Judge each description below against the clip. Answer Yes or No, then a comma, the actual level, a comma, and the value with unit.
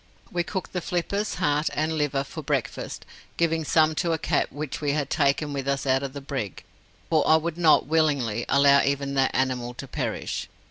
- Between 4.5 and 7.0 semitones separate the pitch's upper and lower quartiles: No, narrow, 2.6 semitones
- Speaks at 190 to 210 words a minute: Yes, average, 195 wpm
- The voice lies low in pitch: No, medium, 145 Hz